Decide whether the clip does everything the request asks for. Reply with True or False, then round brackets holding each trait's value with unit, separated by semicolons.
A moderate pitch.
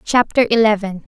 False (215 Hz)